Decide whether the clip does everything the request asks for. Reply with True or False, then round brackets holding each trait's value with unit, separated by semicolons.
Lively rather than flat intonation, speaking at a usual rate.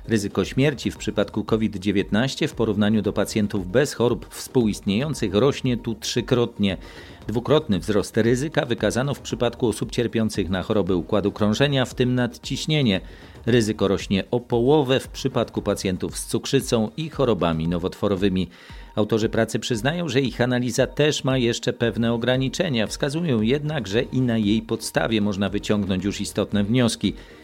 False (3.7 semitones; 140 wpm)